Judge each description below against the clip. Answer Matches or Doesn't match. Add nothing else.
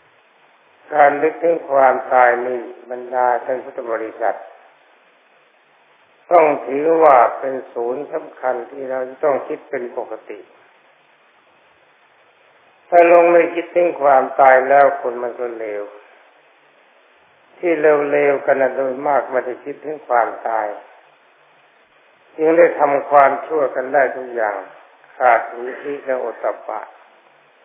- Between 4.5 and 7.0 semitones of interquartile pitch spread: Doesn't match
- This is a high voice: Doesn't match